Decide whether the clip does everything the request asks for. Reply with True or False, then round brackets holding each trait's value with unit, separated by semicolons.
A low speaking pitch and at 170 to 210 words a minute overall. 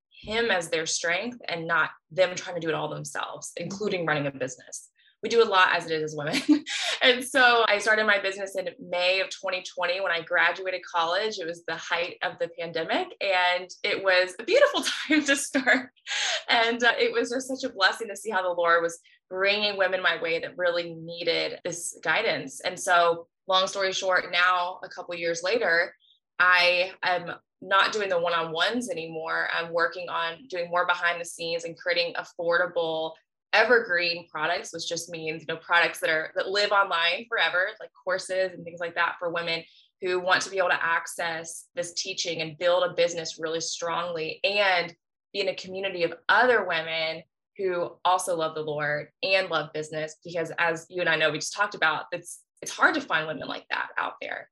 False (175 Hz; 200 wpm)